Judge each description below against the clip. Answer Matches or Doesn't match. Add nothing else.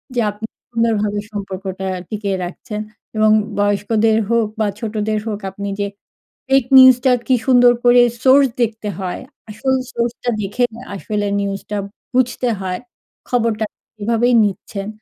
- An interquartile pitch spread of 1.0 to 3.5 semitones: Matches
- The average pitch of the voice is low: Doesn't match